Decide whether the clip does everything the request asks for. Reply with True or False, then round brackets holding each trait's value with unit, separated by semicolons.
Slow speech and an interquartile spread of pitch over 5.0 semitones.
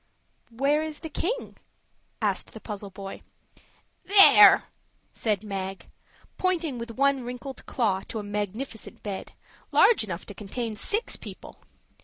True (130 wpm; 5.6 semitones)